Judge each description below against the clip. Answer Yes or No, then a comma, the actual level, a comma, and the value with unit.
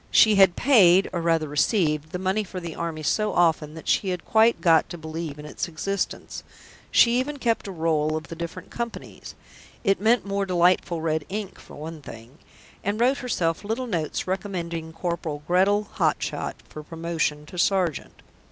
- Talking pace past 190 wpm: No, average, 175 wpm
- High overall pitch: No, medium, 175 Hz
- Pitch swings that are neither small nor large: Yes, average, 3.9 semitones